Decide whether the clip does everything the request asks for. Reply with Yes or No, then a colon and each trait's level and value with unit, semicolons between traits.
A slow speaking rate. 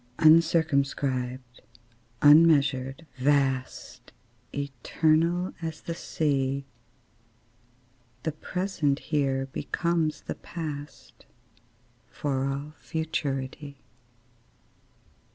Yes: slow, 65 wpm